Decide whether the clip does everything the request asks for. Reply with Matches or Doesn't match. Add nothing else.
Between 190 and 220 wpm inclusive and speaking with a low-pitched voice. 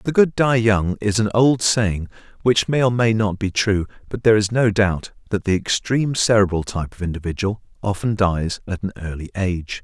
Matches